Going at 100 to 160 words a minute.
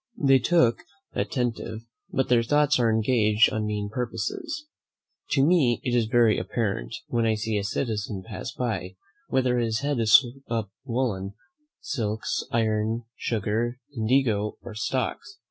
Yes: average, 140 wpm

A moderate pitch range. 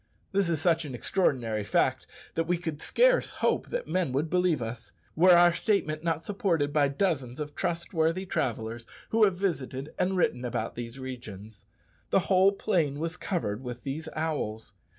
No: wide, 5.9 semitones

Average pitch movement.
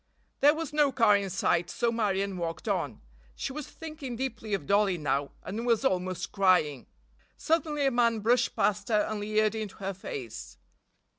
Yes: average, 4.7 semitones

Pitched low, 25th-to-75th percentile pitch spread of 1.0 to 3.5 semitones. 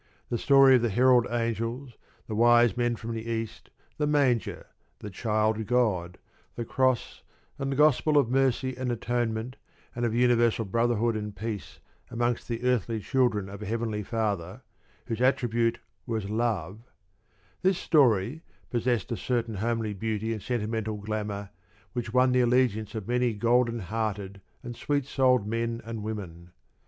Yes: low, 115 Hz; narrow, 2.4 semitones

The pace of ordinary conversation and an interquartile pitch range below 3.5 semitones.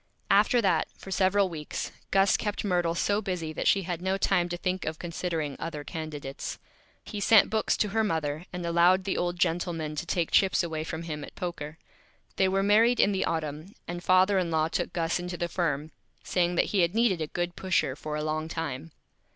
No: fast, 210 wpm; average, 3.1 semitones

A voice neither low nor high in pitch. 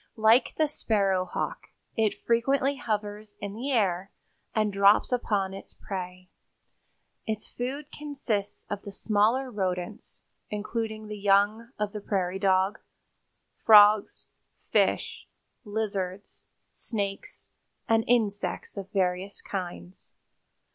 No: high, 205 Hz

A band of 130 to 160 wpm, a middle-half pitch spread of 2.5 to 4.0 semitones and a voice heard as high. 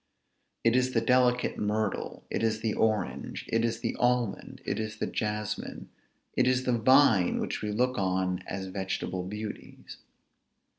No: average, 155 wpm; average, 3.0 semitones; low, 110 Hz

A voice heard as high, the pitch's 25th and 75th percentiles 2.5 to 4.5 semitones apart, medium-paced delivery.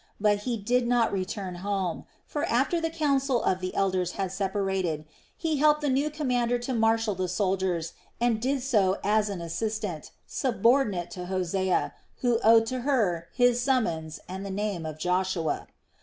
No: high, 210 Hz; average, 4.9 semitones; average, 165 wpm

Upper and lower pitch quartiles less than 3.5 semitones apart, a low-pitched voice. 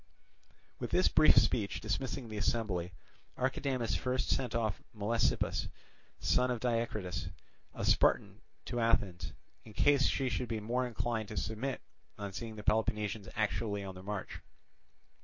Yes: average, 2.9 semitones; low, 110 Hz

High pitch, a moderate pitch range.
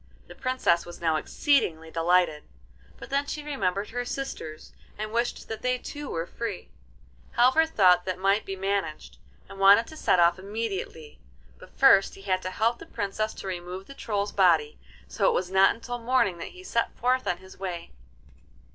Yes: high, 195 Hz; average, 5.0 semitones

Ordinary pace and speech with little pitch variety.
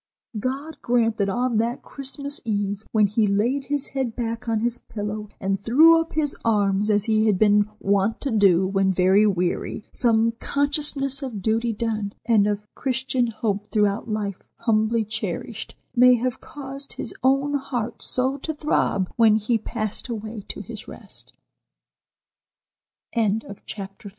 No: average, 155 wpm; average, 3.8 semitones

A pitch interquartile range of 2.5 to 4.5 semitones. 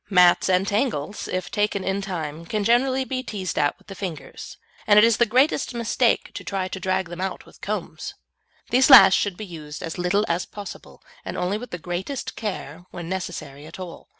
Yes: average, 3.3 semitones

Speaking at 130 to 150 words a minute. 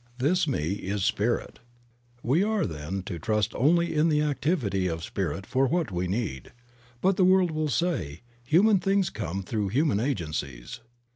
No: average, 160 wpm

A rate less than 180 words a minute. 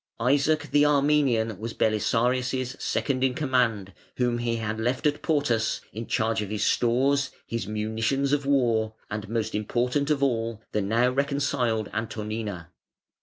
Yes: average, 145 wpm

